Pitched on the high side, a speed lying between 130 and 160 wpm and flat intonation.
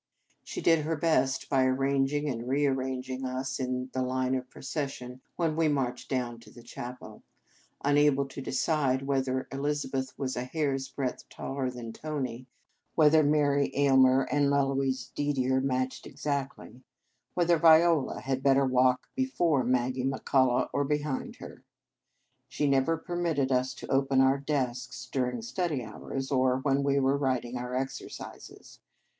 No: low, 135 Hz; average, 150 wpm; narrow, 2.0 semitones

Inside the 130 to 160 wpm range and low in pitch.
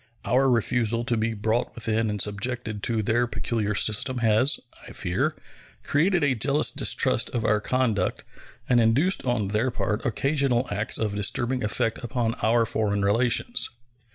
Yes: average, 155 wpm; low, 115 Hz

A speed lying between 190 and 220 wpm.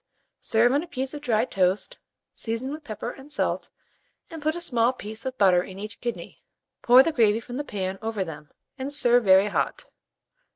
Yes: average, 195 wpm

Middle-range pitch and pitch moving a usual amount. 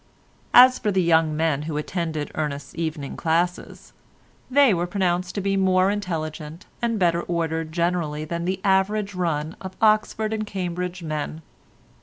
Yes: medium, 175 Hz; average, 3.3 semitones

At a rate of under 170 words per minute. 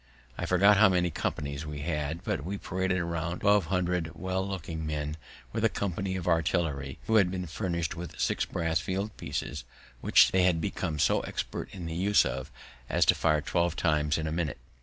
No: average, 195 wpm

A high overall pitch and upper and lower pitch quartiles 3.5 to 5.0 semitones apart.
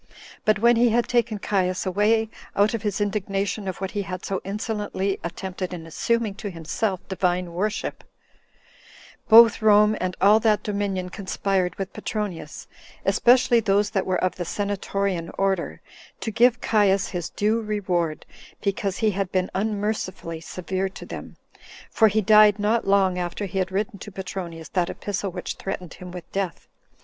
No: high, 195 Hz; narrow, 2.4 semitones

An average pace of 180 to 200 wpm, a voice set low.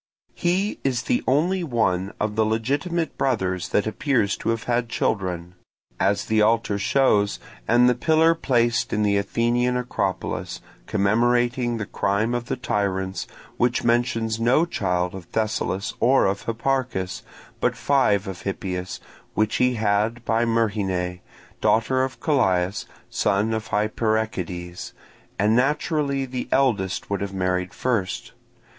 No: slow, 135 wpm; low, 115 Hz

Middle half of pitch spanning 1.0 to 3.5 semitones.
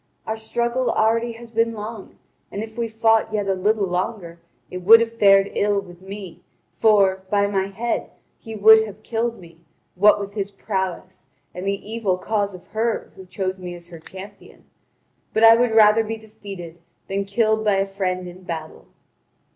Yes: average, 2.7 semitones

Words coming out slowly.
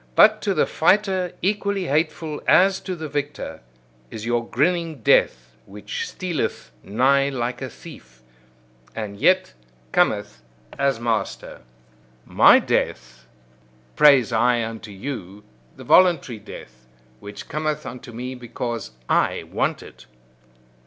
Yes: slow, 120 wpm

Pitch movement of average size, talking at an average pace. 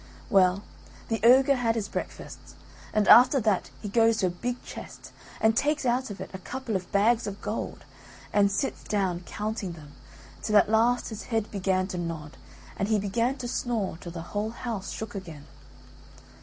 Yes: average, 3.6 semitones; average, 185 wpm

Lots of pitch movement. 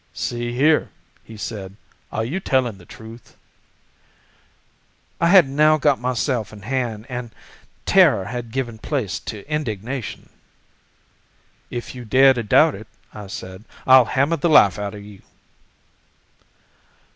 No: average, 4.1 semitones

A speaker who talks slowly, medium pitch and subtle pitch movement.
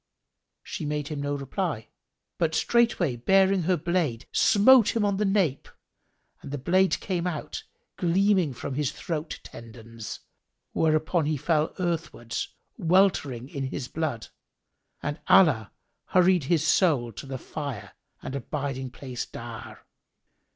No: slow, 130 wpm; medium, 155 Hz; average, 5.3 semitones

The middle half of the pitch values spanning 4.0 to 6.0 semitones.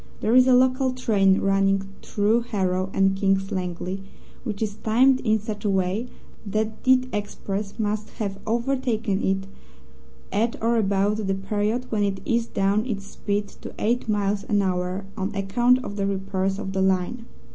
No: average, 2.8 semitones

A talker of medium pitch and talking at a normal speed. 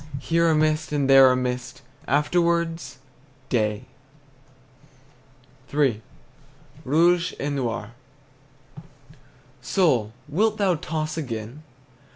No: medium, 145 Hz; slow, 90 wpm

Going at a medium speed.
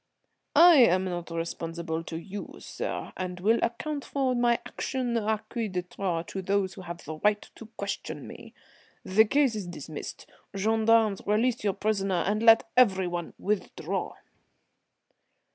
Yes: average, 145 wpm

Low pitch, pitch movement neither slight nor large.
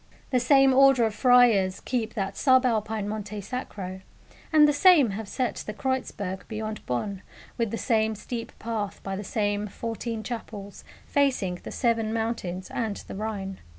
No: high, 220 Hz; average, 3.4 semitones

